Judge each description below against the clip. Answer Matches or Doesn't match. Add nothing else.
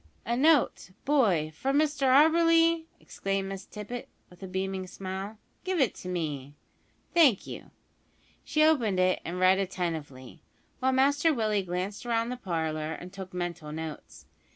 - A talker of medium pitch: Doesn't match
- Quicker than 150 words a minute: Doesn't match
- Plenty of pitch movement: Matches